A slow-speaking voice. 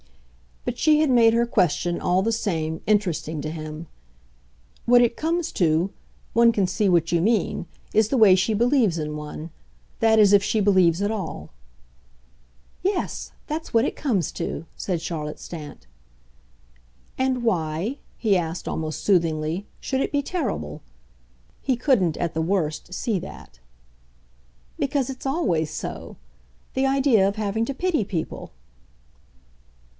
No: average, 145 wpm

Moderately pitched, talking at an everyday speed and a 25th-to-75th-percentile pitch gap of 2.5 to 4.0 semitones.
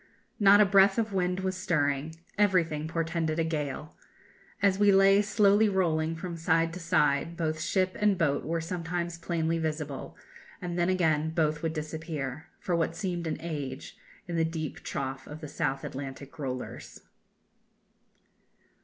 Yes: medium, 165 Hz; average, 155 wpm; average, 3.2 semitones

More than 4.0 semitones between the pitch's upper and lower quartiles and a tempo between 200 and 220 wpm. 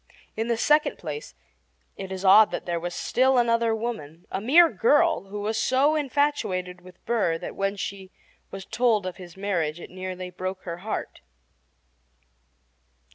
No: average, 4.5 semitones; average, 160 wpm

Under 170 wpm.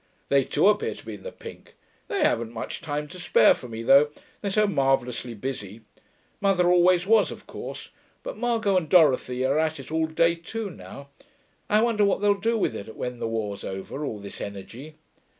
No: average, 200 wpm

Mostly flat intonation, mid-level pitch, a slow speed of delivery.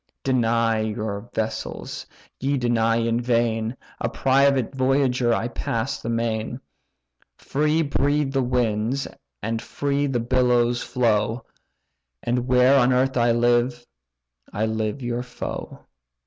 No: narrow, 2.3 semitones; low, 120 Hz; slow, 120 wpm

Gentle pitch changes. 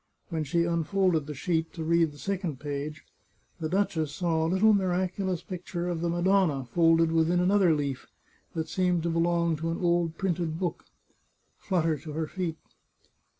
Yes: narrow, 2.1 semitones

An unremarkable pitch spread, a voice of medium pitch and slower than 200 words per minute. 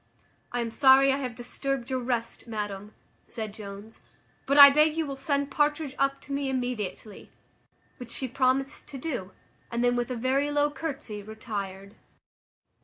No: average, 3.7 semitones; very high, 255 Hz; average, 165 wpm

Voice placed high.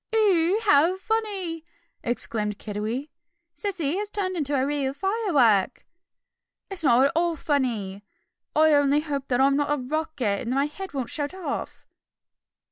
Yes: very high, 290 Hz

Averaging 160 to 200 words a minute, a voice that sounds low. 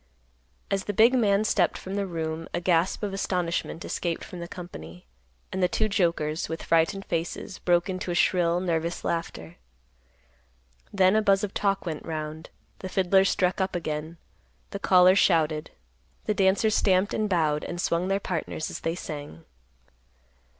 No: average, 165 wpm; medium, 180 Hz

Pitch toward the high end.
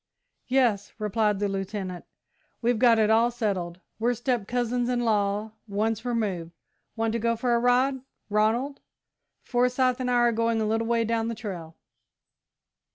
Yes: high, 225 Hz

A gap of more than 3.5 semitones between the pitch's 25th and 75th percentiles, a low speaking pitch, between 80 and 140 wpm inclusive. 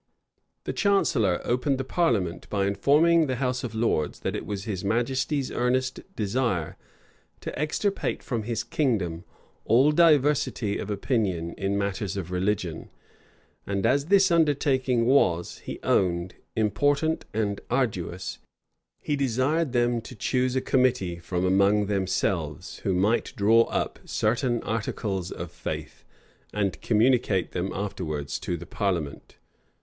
Yes: wide, 5.4 semitones; low, 110 Hz; slow, 135 wpm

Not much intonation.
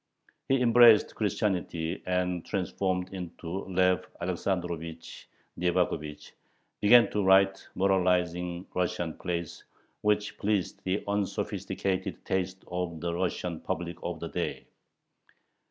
Yes: narrow, 2.0 semitones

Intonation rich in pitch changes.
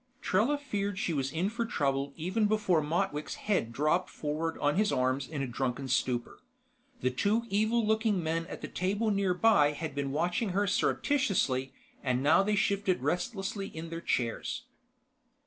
Yes: wide, 6.3 semitones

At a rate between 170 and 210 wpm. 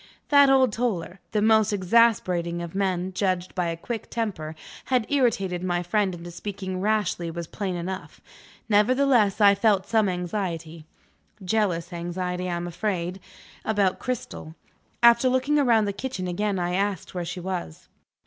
No: average, 150 wpm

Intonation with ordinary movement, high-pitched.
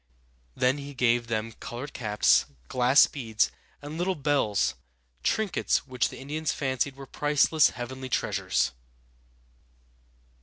No: average, 3.3 semitones; low, 130 Hz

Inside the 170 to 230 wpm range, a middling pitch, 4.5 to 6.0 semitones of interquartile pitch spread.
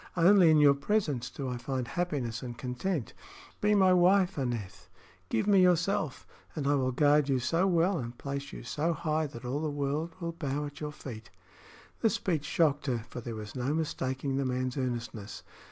Yes: average, 190 wpm; medium, 145 Hz; average, 4.9 semitones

